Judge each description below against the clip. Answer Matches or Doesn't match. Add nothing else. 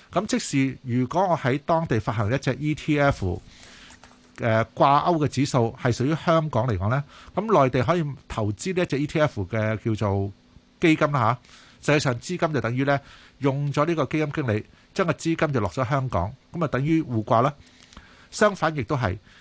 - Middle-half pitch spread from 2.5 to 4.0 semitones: Doesn't match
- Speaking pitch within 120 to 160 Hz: Matches